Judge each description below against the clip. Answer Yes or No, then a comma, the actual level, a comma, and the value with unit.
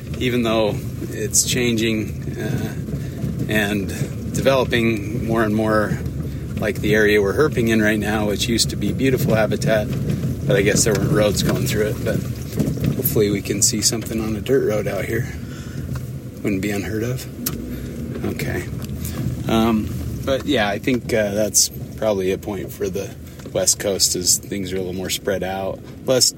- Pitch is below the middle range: Yes, low, 110 Hz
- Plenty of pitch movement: No, narrow, 2.4 semitones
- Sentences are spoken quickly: No, average, 165 wpm